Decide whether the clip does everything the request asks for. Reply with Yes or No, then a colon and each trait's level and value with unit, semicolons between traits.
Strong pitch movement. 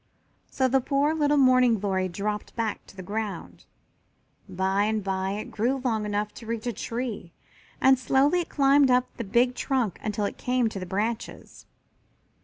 No: average, 4.0 semitones